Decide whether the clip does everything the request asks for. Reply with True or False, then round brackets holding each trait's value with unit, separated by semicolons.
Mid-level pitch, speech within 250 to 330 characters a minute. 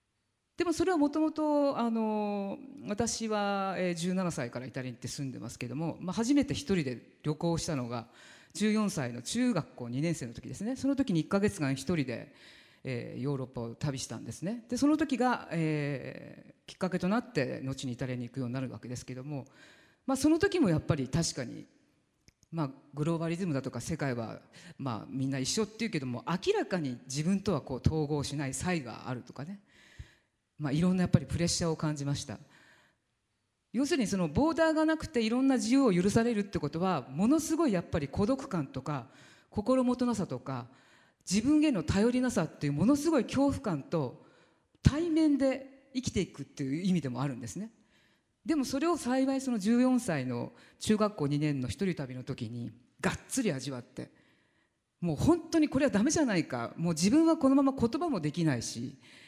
False (170 Hz; 360 characters per minute)